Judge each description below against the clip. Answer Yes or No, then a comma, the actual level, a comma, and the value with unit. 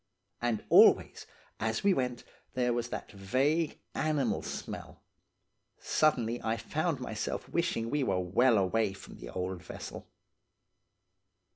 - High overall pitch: No, low, 120 Hz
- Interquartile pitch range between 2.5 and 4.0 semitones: No, average, 4.5 semitones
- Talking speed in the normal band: No, slow, 125 wpm